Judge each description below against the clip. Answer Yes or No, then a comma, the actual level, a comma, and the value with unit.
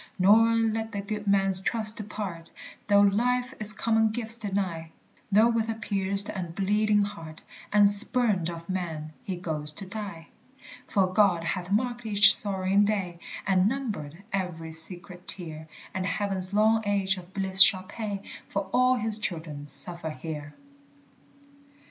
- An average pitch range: Yes, average, 3.3 semitones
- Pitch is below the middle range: No, high, 200 Hz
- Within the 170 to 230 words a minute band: No, average, 150 wpm